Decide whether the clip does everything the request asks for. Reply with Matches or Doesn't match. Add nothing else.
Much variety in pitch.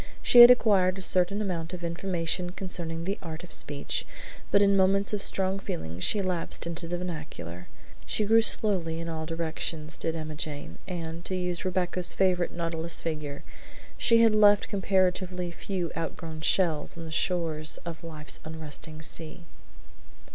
Doesn't match